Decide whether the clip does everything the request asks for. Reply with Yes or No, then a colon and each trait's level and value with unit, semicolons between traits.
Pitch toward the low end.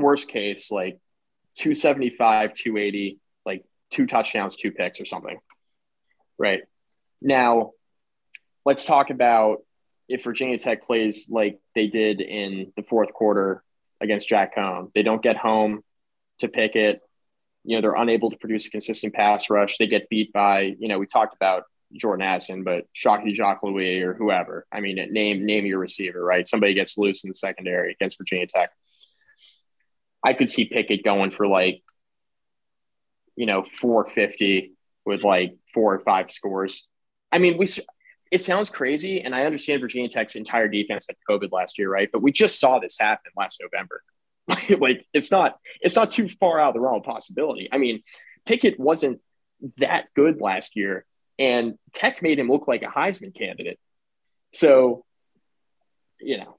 Yes: low, 110 Hz